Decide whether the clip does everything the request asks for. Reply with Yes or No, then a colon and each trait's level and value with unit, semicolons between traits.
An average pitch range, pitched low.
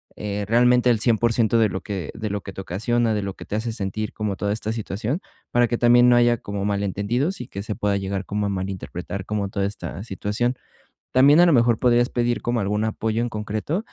Yes: average, 3.1 semitones; low, 110 Hz